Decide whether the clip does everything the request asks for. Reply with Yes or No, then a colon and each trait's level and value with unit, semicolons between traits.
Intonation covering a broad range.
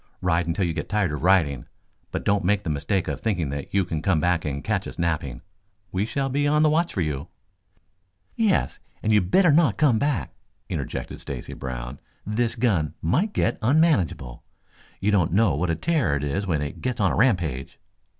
Yes: wide, 7.2 semitones